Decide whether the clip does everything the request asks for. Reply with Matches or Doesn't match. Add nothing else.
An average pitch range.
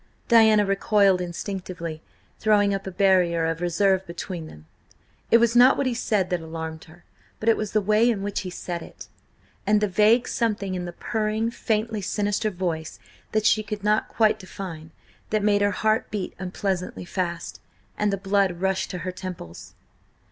Matches